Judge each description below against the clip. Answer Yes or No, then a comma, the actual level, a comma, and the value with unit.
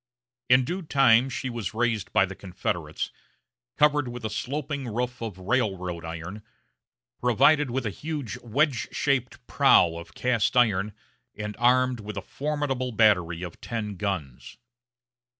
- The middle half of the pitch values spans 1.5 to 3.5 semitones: No, average, 4.9 semitones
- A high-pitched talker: No, low, 115 Hz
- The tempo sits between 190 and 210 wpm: No, average, 140 wpm